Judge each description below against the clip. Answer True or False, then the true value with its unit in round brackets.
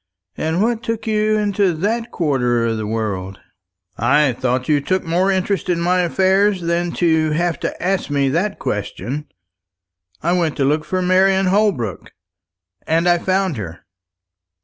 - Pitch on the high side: False (170 Hz)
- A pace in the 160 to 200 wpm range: False (150 wpm)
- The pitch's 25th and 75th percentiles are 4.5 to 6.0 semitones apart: True (5.6 semitones)